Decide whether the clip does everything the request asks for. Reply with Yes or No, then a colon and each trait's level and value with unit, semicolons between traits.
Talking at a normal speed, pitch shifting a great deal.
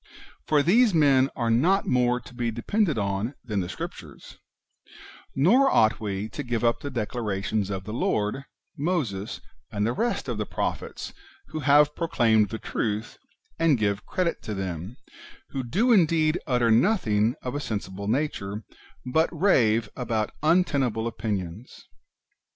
Yes: average, 150 wpm; wide, 5.9 semitones